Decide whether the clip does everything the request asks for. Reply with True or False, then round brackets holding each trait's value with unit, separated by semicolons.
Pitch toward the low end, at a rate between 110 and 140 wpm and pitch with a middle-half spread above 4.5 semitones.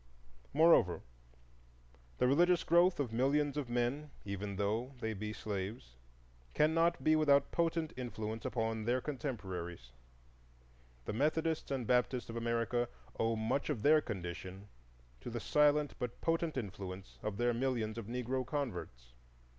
True (120 Hz; 135 wpm; 5.4 semitones)